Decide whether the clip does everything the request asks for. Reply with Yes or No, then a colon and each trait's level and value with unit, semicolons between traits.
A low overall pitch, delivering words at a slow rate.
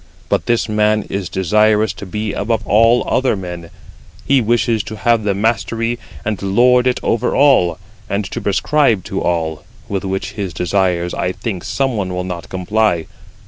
No: low, 105 Hz; average, 170 wpm